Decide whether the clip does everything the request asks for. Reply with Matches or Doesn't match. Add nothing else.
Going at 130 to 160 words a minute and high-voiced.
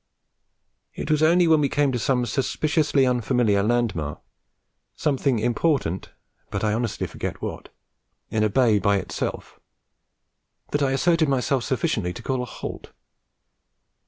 Doesn't match